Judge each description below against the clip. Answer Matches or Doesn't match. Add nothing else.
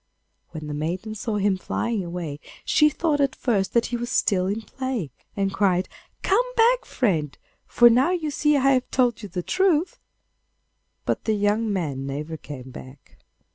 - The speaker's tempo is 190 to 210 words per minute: Doesn't match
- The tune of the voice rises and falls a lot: Matches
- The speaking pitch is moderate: Doesn't match